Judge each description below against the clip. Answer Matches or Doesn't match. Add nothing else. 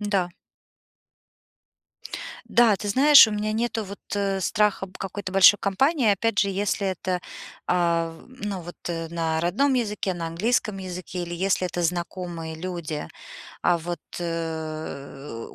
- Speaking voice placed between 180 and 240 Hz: Matches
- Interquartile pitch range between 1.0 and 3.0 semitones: Doesn't match